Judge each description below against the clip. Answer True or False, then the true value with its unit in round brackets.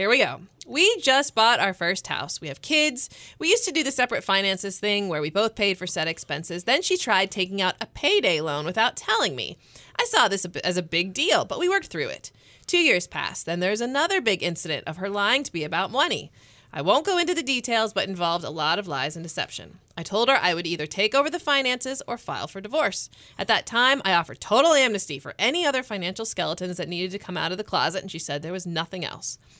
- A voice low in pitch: False (195 Hz)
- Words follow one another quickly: True (245 wpm)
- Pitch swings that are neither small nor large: False (7.4 semitones)